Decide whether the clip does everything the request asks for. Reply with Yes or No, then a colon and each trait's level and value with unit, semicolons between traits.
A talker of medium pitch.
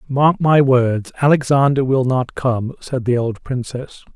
No: low, 130 Hz